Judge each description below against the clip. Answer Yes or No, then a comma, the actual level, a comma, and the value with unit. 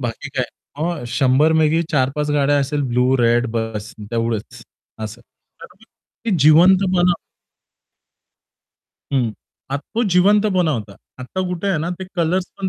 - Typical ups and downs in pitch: No, wide, 6.5 semitones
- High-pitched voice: No, medium, 150 Hz